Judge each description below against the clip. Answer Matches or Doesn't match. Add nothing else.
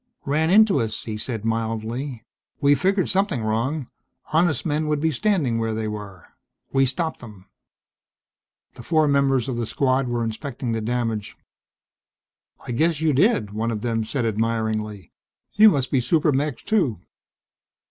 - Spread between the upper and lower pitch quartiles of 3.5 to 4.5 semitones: Doesn't match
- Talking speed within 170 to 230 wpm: Doesn't match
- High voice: Doesn't match